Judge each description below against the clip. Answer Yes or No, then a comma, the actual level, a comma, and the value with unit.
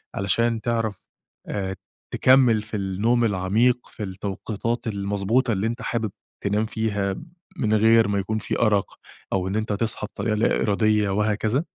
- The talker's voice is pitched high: No, low, 105 Hz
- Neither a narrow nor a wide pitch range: No, narrow, 2.3 semitones